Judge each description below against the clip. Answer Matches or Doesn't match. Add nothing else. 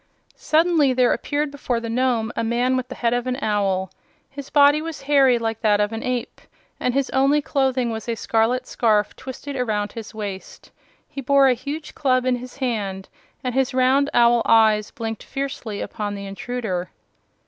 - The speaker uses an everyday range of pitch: Matches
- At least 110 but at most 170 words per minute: Doesn't match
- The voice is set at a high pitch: Matches